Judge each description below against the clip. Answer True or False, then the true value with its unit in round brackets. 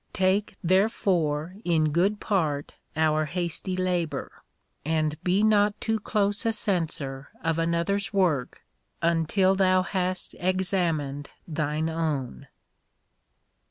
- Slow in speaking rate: True (105 wpm)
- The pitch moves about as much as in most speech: True (3.7 semitones)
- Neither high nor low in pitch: True (175 Hz)